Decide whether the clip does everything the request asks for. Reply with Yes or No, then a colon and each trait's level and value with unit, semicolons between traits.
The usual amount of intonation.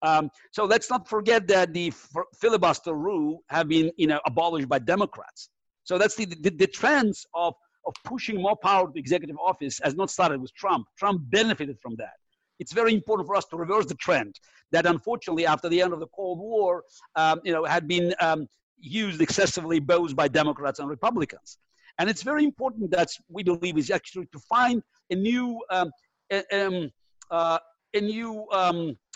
Yes: average, 4.4 semitones